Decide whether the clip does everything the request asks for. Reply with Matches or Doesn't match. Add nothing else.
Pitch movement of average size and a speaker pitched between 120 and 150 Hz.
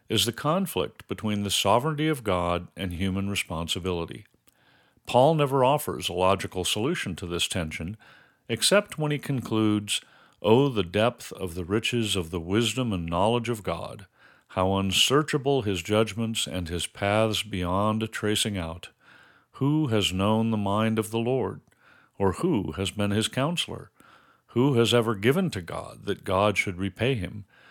Doesn't match